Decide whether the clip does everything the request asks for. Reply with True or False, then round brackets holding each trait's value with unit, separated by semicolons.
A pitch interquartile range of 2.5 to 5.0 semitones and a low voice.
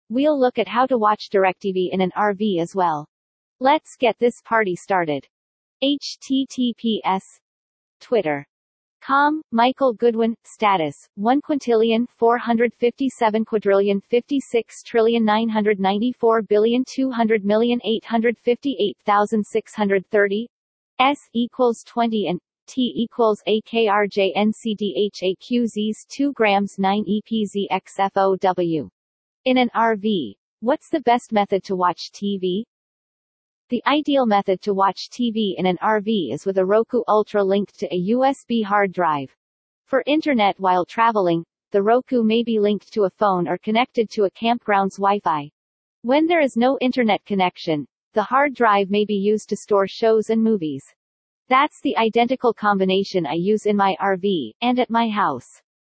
False (3.4 semitones; 215 Hz)